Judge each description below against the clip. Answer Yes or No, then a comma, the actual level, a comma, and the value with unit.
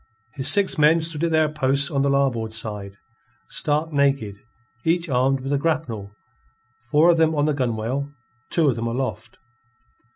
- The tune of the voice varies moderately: Yes, average, 4.1 semitones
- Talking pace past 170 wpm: No, average, 165 wpm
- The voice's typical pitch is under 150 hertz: Yes, medium, 140 Hz